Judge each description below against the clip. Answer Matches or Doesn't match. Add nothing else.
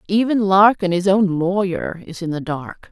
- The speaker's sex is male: Doesn't match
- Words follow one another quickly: Doesn't match